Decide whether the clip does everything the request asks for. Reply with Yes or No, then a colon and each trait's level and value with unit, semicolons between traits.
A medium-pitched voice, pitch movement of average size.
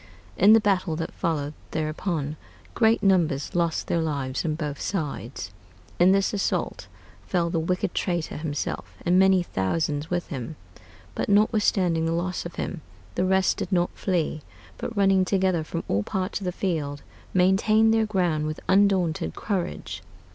Yes: medium, 175 Hz; average, 3.7 semitones